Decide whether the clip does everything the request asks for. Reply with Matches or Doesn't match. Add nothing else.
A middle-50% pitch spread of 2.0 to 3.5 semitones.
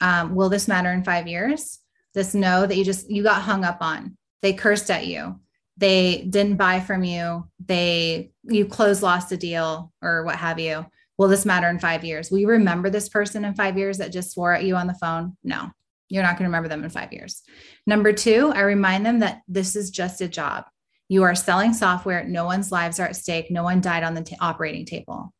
Matches